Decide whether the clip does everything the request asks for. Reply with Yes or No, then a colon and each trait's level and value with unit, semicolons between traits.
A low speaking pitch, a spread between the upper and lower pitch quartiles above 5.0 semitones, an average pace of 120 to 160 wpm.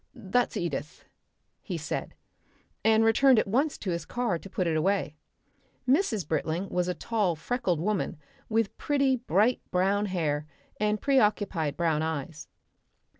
No: high, 195 Hz; wide, 5.5 semitones; average, 140 wpm